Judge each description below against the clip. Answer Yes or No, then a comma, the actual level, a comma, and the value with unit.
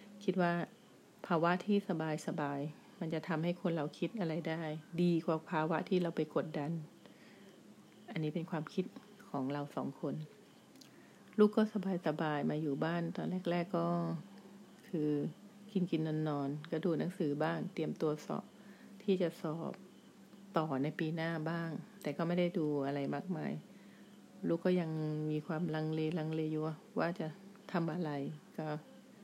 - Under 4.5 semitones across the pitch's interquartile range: Yes, average, 3.3 semitones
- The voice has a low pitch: No, medium, 165 Hz